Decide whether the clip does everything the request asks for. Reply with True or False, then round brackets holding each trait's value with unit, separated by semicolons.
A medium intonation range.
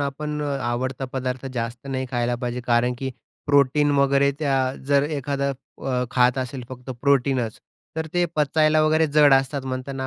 False (2.1 semitones)